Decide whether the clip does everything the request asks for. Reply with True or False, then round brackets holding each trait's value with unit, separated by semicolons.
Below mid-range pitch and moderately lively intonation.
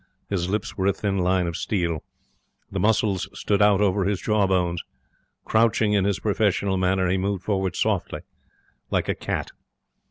False (95 Hz; 2.0 semitones)